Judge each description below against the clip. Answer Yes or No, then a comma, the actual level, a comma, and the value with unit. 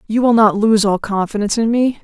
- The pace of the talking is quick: Yes, fast, 235 wpm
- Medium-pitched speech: No, high, 215 Hz